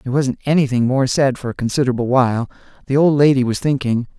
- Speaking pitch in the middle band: No, low, 130 Hz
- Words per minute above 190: Yes, average, 200 wpm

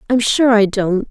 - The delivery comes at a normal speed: No, fast, 220 wpm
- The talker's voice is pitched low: No, high, 220 Hz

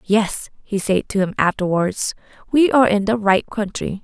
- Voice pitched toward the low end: No, high, 205 Hz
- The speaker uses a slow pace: No, average, 180 wpm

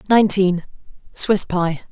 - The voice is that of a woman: Yes, female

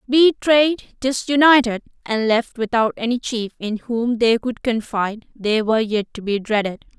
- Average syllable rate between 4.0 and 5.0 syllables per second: Yes, 4.6 syllables/s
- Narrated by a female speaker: Yes, female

